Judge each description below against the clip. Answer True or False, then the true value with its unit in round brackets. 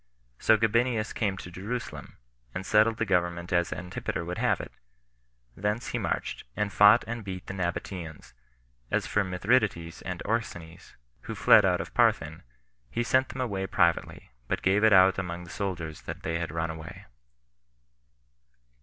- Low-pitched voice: True (95 Hz)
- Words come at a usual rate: True (160 wpm)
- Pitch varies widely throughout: False (3.8 semitones)